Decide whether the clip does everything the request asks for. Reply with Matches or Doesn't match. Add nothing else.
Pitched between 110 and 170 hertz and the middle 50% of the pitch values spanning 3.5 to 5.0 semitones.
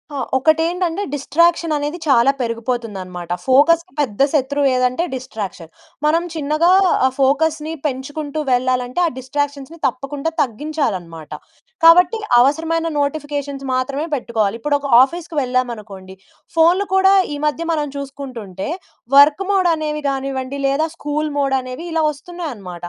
Doesn't match